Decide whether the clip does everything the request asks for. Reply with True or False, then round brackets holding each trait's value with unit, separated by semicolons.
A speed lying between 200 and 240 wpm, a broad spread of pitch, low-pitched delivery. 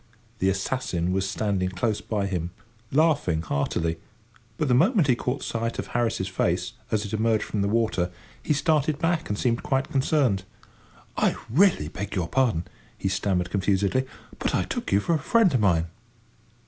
False (175 wpm; 6.0 semitones; 110 Hz)